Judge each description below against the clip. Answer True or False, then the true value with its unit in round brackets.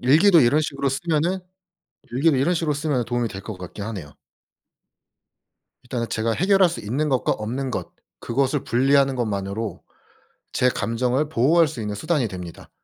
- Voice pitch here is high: False (130 Hz)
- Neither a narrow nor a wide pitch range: True (5.0 semitones)